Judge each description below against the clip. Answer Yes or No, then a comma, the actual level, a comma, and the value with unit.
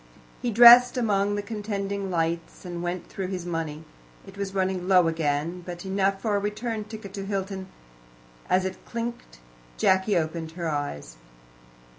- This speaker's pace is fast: No, average, 155 wpm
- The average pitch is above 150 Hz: Yes, high, 190 Hz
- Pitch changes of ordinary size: Yes, average, 3.1 semitones